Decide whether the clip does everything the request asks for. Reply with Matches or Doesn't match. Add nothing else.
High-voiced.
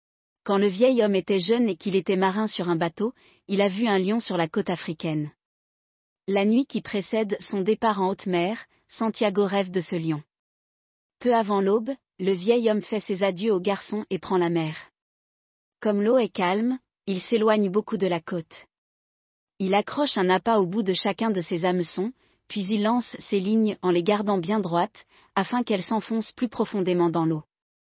Matches